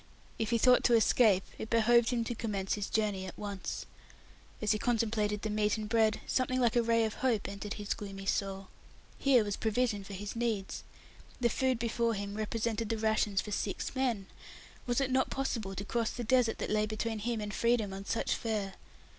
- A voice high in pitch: Yes, high, 220 Hz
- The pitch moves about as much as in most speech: No, narrow, 2.3 semitones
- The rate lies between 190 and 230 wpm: Yes, average, 200 wpm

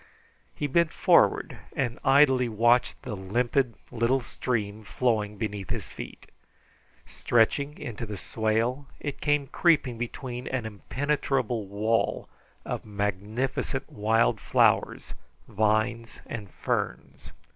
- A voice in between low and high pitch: No, low, 115 Hz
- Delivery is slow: Yes, slow, 110 wpm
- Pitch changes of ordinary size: Yes, average, 3.6 semitones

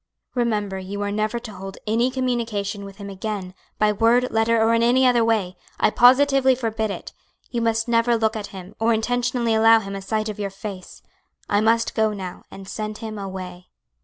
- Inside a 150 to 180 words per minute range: No, average, 195 wpm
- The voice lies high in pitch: Yes, high, 220 Hz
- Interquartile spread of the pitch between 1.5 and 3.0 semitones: Yes, average, 2.7 semitones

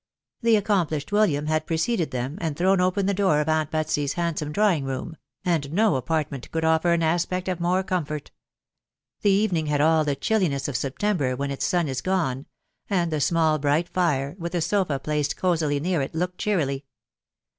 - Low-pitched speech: No, medium, 160 Hz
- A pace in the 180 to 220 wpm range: Yes, average, 185 wpm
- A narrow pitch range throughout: No, average, 4.0 semitones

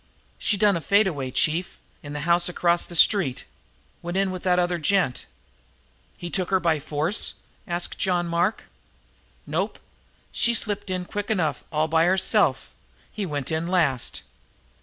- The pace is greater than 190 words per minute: No, average, 160 wpm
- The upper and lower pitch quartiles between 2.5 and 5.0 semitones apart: Yes, average, 3.2 semitones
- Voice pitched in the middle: Yes, medium, 175 Hz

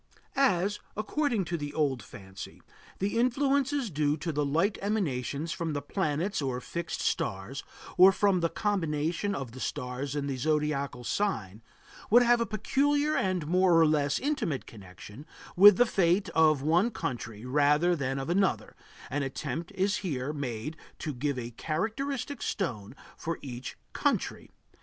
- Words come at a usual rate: Yes, average, 150 wpm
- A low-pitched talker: No, medium, 160 Hz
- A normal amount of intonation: No, wide, 6.4 semitones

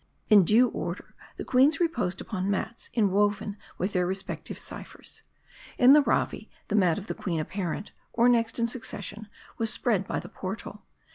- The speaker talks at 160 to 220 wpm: Yes, average, 165 wpm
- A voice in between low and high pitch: No, high, 210 Hz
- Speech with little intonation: No, average, 3.6 semitones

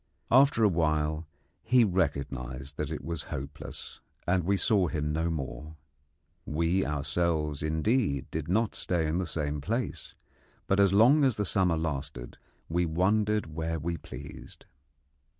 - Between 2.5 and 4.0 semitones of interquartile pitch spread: No, average, 4.4 semitones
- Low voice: Yes, very low, 80 Hz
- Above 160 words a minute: No, average, 145 wpm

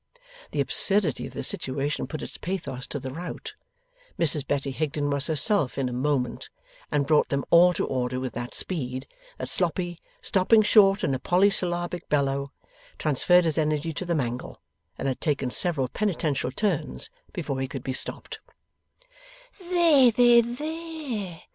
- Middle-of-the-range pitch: Yes, medium, 155 Hz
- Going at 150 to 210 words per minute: Yes, average, 155 wpm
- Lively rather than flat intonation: Yes, wide, 5.8 semitones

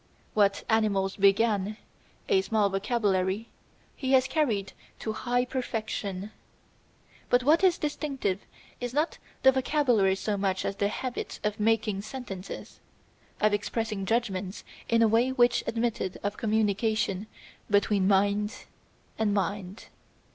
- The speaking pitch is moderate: No, high, 215 Hz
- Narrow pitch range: No, average, 3.5 semitones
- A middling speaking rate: No, slow, 125 wpm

